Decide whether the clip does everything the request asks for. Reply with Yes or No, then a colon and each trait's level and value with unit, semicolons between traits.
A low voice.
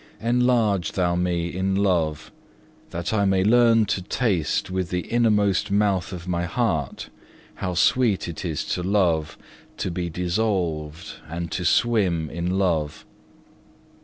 Yes: very low, 90 Hz